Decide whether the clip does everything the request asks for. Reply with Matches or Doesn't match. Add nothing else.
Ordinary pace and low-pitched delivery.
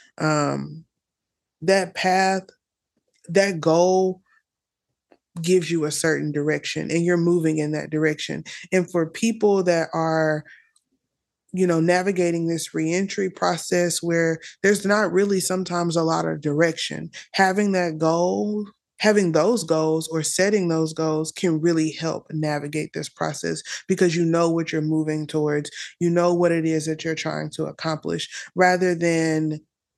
Doesn't match